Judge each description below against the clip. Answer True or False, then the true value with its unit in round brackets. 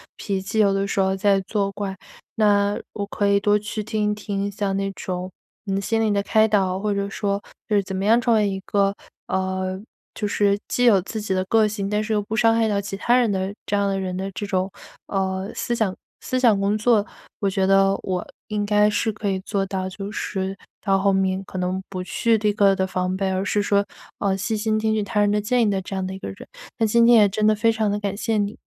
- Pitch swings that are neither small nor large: False (1.7 semitones)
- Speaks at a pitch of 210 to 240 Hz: False (200 Hz)